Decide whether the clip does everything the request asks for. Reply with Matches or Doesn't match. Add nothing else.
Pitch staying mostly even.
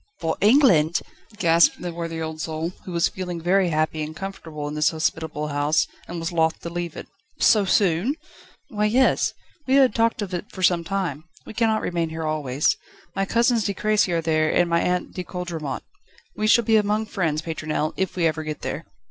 Doesn't match